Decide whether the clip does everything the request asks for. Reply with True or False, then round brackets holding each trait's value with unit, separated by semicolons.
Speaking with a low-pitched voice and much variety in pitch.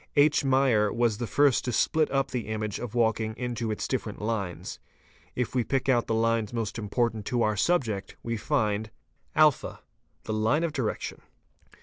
False (115 Hz; 3.2 semitones)